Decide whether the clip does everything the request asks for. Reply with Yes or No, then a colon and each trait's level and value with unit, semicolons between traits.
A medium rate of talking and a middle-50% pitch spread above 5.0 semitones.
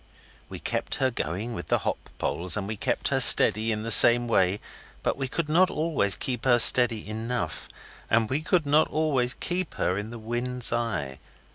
No: average, 190 wpm; average, 3.8 semitones